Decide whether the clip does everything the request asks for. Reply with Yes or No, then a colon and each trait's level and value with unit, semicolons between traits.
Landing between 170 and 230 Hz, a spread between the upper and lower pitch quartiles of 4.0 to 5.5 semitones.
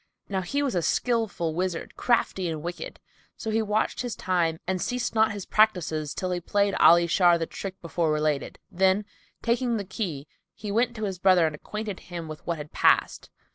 Yes: medium, 185 Hz; average, 4.4 semitones